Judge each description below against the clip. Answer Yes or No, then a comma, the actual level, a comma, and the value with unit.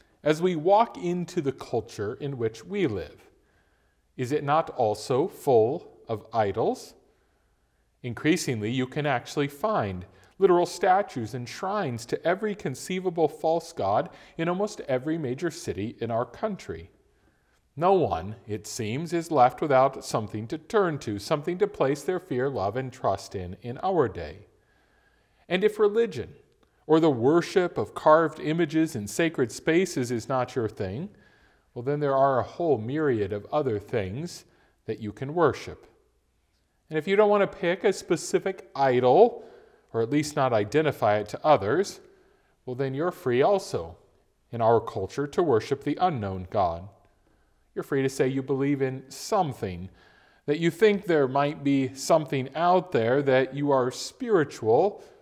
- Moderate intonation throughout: No, wide, 6.3 semitones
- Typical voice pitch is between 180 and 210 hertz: No, medium, 140 Hz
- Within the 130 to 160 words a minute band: Yes, average, 155 wpm